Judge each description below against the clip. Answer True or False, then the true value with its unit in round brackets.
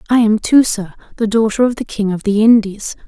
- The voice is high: True (215 Hz)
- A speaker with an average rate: False (215 wpm)